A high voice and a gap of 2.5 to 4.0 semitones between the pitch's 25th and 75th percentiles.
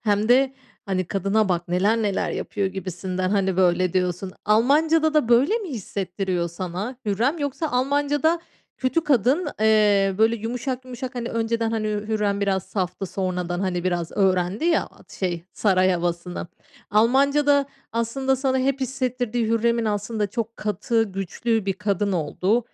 No: high, 215 Hz; average, 5.1 semitones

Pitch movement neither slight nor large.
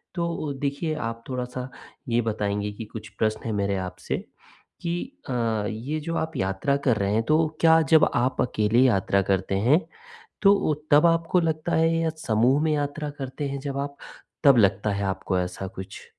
No: wide, 6.6 semitones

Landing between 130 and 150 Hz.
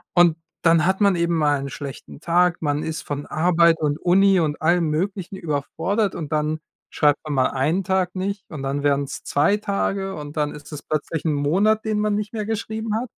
No: medium, 165 Hz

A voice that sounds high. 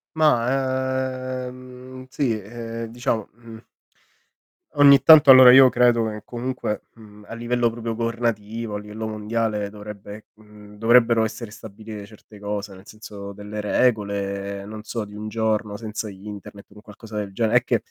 No: low, 110 Hz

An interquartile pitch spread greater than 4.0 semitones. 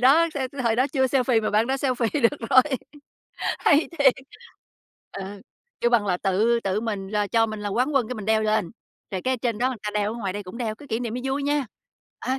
No: average, 3.7 semitones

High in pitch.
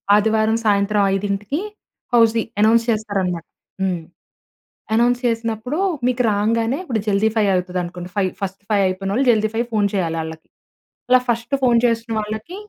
Yes: high, 215 Hz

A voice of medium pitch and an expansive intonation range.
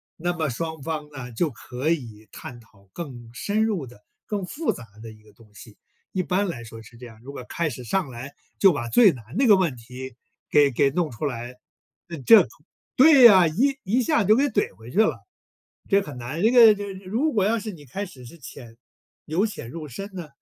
Yes: medium, 155 Hz; wide, 8.7 semitones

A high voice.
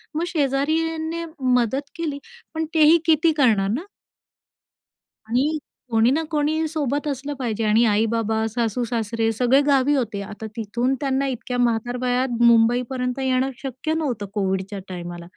Yes: very high, 250 Hz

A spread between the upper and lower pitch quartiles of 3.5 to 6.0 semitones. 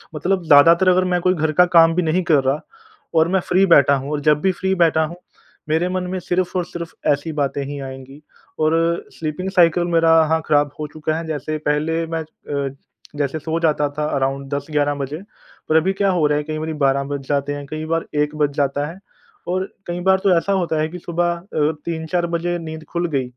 No: average, 3.1 semitones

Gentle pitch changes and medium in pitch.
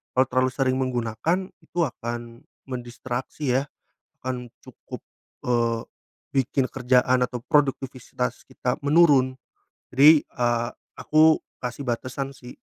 No: narrow, 2.1 semitones; low, 130 Hz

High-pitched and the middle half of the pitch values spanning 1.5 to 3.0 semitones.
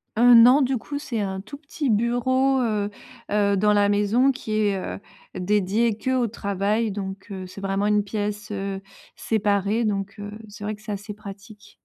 Yes: high, 210 Hz; narrow, 2.5 semitones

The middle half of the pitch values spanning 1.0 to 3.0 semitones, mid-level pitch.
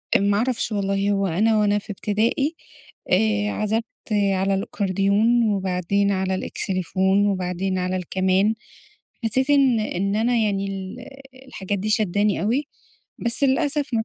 No: narrow, 2.6 semitones; high, 205 Hz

